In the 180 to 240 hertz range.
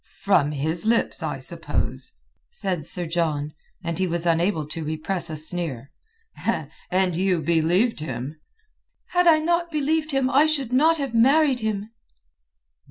Yes: medium, 185 Hz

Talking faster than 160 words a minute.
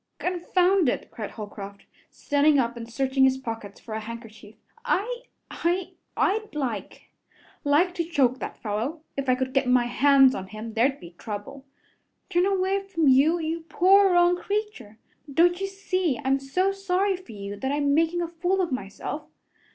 Yes: average, 170 wpm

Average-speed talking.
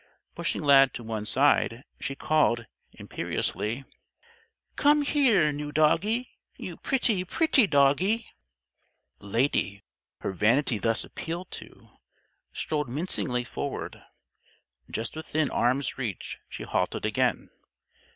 No: slow, 105 wpm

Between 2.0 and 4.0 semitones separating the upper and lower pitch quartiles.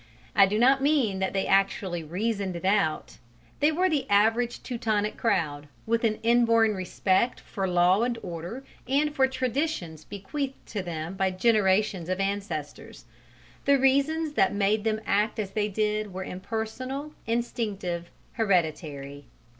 No: average, 4.4 semitones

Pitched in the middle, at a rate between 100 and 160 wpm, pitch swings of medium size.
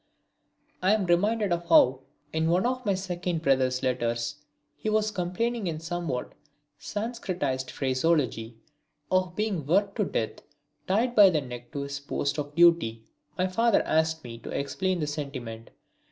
No: medium, 170 Hz; average, 155 wpm; wide, 6.0 semitones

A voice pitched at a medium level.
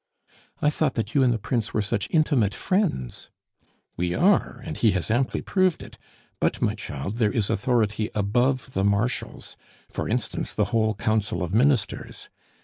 No: low, 110 Hz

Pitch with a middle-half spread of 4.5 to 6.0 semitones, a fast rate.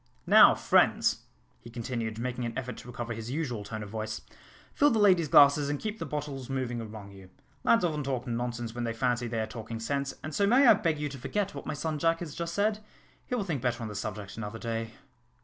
Yes: average, 5.1 semitones; fast, 235 wpm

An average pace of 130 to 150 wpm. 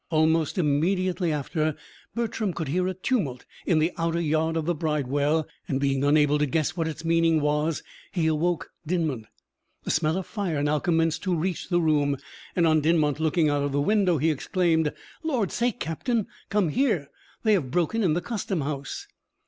No: average, 180 wpm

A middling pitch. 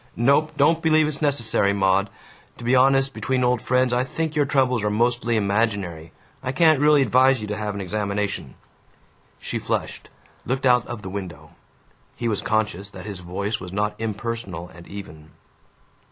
No: low, 110 Hz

